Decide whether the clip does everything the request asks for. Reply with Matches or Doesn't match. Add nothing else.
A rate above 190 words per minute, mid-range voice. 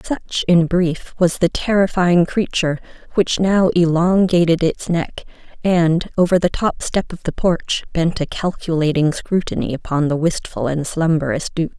Doesn't match